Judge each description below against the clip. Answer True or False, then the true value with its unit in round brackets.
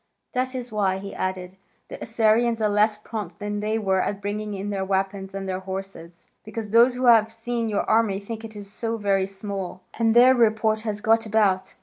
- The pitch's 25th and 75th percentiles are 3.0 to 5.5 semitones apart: False (2.6 semitones)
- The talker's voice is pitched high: True (210 Hz)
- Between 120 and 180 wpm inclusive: False (200 wpm)